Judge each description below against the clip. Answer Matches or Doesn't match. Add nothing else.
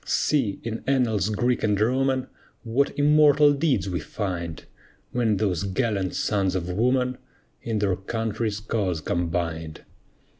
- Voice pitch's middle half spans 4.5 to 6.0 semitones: Matches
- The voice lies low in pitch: Matches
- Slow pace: Matches